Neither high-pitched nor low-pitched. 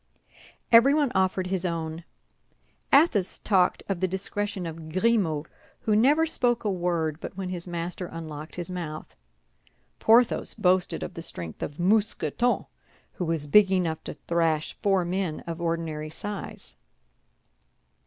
Yes: medium, 180 Hz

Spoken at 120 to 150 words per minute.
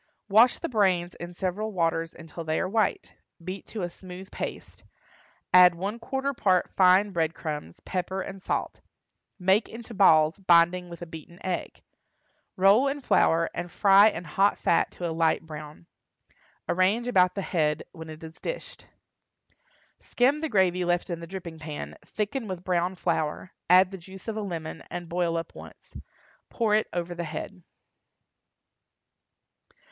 No: average, 160 wpm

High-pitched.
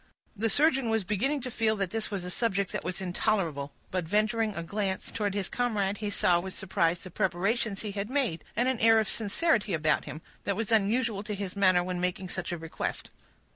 Yes: high, 200 Hz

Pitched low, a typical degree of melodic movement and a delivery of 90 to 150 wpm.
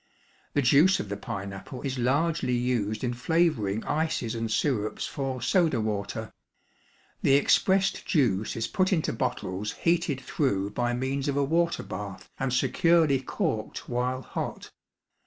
No: low, 130 Hz; wide, 5.8 semitones; average, 140 wpm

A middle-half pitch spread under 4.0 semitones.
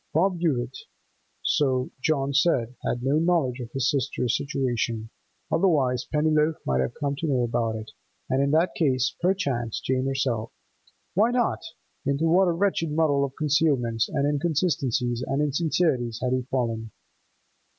No: average, 4.5 semitones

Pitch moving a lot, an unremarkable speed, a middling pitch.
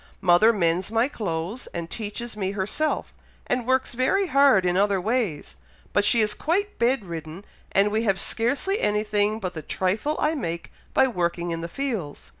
No: wide, 5.7 semitones; average, 175 wpm; high, 210 Hz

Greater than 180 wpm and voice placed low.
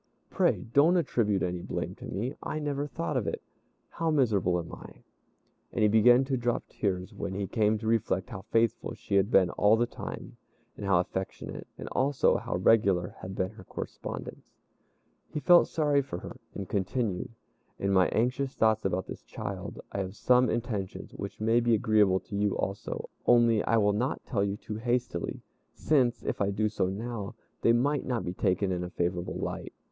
Yes: average, 190 wpm; low, 110 Hz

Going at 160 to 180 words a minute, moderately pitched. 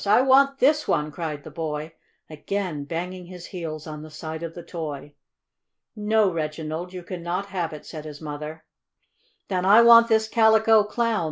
Yes: average, 170 wpm; medium, 175 Hz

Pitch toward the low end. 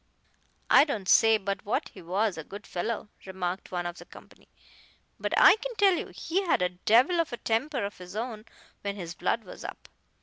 No: high, 210 Hz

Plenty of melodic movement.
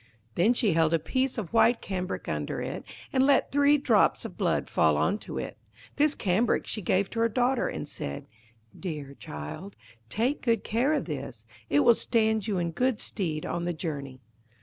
Yes: wide, 7.1 semitones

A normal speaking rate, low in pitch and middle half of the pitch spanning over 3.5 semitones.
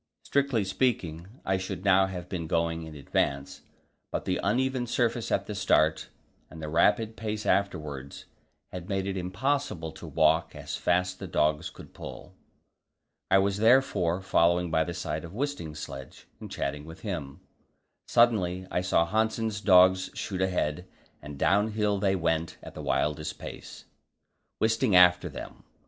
Yes: average, 155 wpm; very low, 95 Hz; average, 4.4 semitones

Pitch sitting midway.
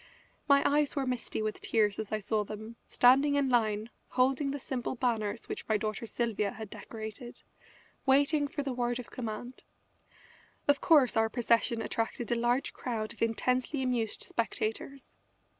No: high, 240 Hz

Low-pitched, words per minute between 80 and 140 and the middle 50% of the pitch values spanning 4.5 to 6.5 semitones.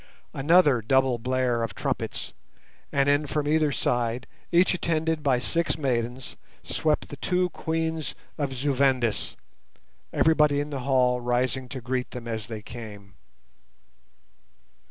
No: low, 130 Hz; slow, 135 wpm; average, 3.7 semitones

